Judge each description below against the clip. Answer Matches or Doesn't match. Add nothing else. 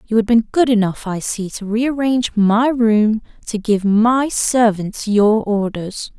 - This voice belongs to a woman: Matches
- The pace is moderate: Matches